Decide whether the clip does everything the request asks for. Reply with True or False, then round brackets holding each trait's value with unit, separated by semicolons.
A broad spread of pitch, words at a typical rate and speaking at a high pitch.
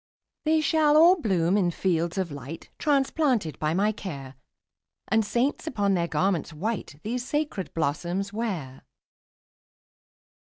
False (7.0 semitones; 125 wpm; 195 Hz)